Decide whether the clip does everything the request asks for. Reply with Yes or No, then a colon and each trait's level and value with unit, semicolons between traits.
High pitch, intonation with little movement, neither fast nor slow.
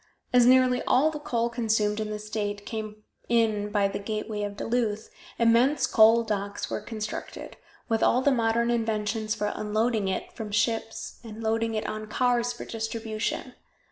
Yes: high, 220 Hz; narrow, 1.8 semitones; average, 165 wpm